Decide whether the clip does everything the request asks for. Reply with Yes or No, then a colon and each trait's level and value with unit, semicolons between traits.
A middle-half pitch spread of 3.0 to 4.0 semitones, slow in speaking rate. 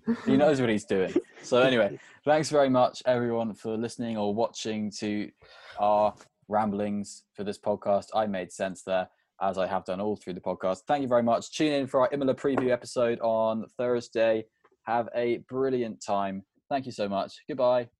No: average, 3.4 semitones; average, 185 wpm